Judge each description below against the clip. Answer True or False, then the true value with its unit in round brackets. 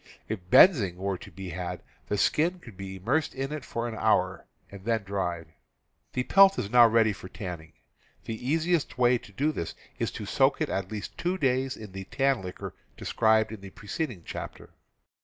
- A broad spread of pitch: True (5.8 semitones)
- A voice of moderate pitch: False (110 Hz)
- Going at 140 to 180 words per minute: False (195 wpm)